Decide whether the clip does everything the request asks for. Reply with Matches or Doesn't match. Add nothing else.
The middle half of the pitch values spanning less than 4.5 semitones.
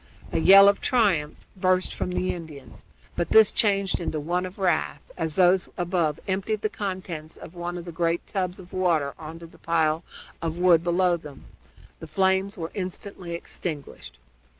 Matches